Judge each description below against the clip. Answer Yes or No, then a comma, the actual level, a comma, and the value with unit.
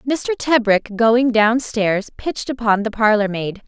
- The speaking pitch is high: Yes, high, 225 Hz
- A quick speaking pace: No, average, 145 wpm